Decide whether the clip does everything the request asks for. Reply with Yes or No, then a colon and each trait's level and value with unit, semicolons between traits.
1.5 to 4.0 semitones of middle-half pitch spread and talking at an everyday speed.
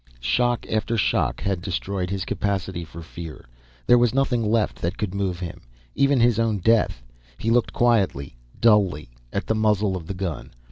No: average, 4.4 semitones; average, 175 wpm